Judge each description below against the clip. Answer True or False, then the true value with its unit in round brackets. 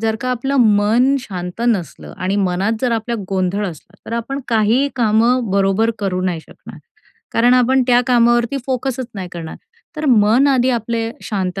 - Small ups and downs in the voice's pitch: False (4.1 semitones)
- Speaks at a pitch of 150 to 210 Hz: False (225 Hz)